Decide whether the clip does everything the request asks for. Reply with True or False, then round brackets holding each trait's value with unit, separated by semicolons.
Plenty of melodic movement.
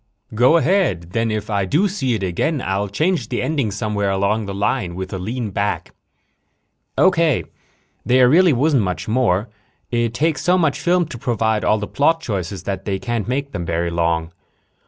True (6.5 semitones)